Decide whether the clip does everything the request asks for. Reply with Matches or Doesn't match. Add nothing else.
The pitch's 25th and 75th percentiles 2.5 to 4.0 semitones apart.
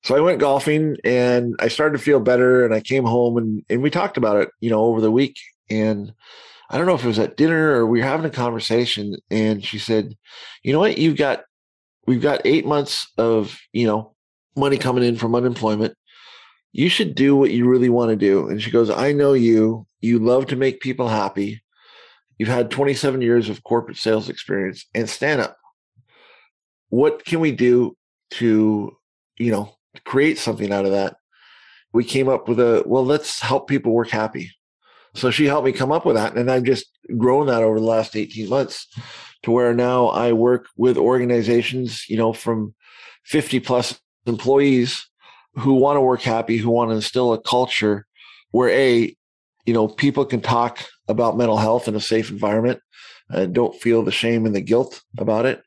Matches